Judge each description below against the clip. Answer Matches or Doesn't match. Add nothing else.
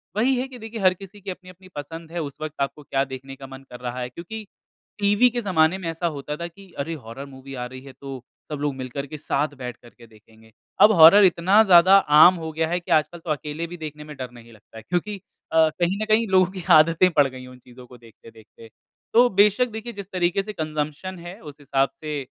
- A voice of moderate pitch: Matches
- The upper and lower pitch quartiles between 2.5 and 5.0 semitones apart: Doesn't match